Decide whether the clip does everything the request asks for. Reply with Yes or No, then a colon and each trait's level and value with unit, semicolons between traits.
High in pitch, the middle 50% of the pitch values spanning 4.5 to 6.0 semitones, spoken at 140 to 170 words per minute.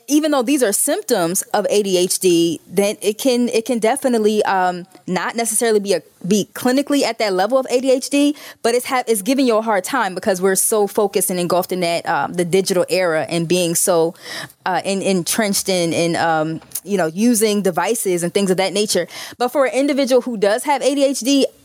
No: high, 205 Hz; wide, 5.5 semitones; average, 200 wpm